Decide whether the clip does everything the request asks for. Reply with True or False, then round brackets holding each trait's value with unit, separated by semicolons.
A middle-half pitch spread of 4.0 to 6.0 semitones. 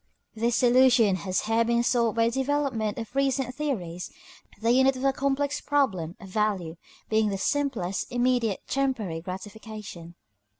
True (5.0 semitones)